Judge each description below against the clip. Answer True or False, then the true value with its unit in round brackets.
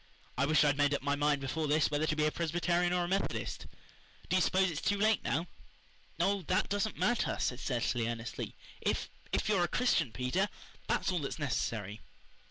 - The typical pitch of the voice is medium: True (155 Hz)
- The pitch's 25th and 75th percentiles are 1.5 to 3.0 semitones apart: False (4.8 semitones)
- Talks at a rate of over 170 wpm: True (200 wpm)